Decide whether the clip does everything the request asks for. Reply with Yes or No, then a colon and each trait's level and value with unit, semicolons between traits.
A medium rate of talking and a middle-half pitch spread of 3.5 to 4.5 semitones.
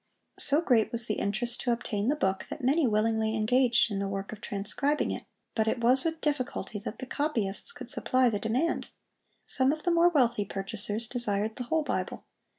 Yes: average, 195 wpm; average, 4.2 semitones